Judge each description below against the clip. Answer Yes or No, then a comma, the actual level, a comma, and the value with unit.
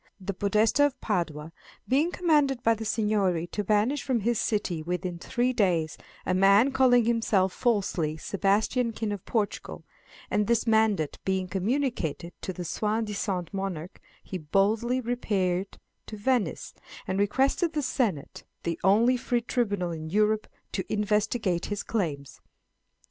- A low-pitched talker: No, high, 210 Hz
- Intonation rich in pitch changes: No, average, 4.3 semitones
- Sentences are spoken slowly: No, average, 145 wpm